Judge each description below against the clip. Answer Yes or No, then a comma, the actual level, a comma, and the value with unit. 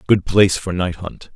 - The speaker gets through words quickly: Yes, fast, 220 wpm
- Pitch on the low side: Yes, very low, 95 Hz